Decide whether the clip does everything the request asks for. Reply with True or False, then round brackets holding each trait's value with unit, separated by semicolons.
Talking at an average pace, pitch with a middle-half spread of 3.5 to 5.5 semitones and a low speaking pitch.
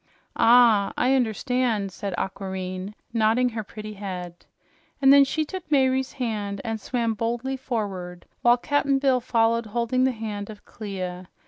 False (145 wpm; 4.1 semitones; 225 Hz)